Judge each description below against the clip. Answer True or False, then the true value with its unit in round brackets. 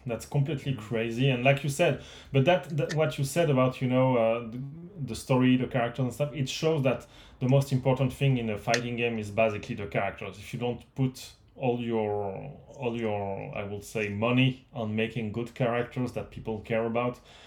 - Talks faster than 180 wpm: True (205 wpm)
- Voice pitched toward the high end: False (125 Hz)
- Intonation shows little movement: False (3.2 semitones)